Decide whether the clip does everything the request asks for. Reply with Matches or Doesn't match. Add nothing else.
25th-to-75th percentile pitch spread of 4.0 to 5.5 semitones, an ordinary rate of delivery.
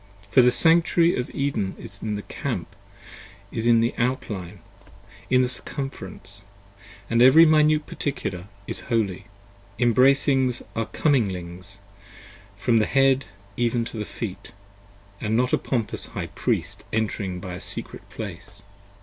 Doesn't match